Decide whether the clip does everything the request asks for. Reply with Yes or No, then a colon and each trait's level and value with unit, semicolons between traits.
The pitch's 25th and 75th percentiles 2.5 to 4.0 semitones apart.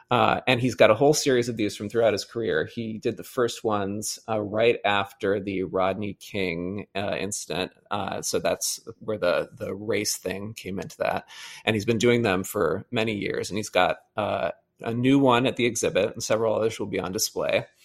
Yes: average, 3.3 semitones